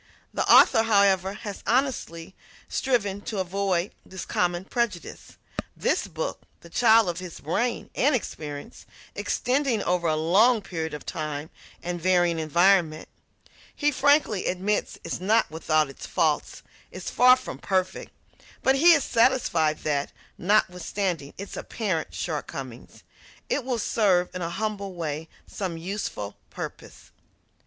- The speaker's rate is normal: No, slow, 130 wpm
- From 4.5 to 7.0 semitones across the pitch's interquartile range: Yes, average, 5.1 semitones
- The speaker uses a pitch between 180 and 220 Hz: Yes, medium, 185 Hz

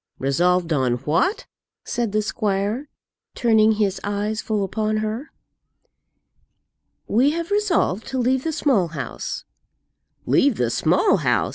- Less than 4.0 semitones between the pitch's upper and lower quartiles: No, average, 5.0 semitones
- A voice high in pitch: Yes, high, 215 Hz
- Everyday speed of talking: No, slow, 125 wpm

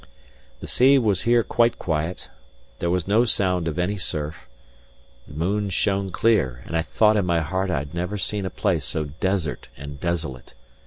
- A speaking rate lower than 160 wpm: No, average, 180 wpm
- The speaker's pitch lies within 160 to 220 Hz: No, very low, 90 Hz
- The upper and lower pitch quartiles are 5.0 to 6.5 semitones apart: No, average, 4.5 semitones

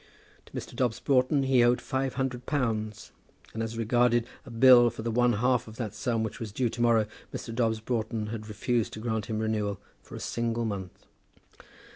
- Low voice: Yes, low, 115 Hz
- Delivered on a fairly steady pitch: Yes, narrow, 2.0 semitones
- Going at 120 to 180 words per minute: No, average, 195 wpm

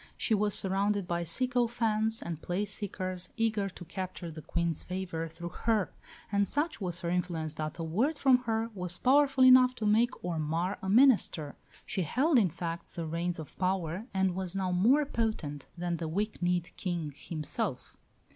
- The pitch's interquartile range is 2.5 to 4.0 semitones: No, average, 4.6 semitones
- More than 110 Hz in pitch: Yes, medium, 185 Hz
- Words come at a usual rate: Yes, average, 175 wpm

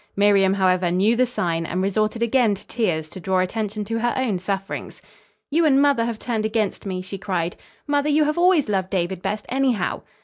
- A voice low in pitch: No, high, 210 Hz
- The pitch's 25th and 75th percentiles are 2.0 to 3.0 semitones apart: No, average, 4.4 semitones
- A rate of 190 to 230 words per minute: Yes, average, 200 wpm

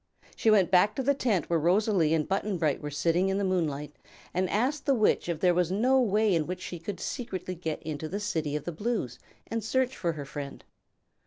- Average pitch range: Yes, average, 5.0 semitones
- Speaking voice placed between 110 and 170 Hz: No, medium, 185 Hz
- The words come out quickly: Yes, fast, 225 wpm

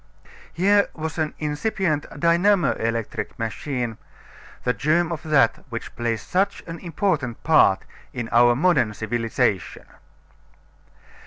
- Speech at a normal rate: No, slow, 110 wpm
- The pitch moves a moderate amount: No, wide, 6.3 semitones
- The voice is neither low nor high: Yes, medium, 150 Hz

